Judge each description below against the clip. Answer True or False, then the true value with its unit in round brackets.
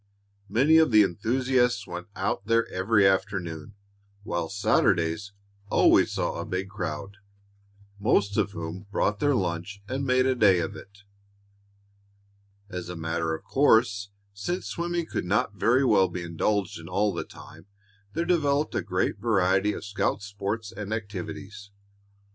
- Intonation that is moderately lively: True (3.8 semitones)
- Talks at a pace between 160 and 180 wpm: False (150 wpm)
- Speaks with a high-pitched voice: False (100 Hz)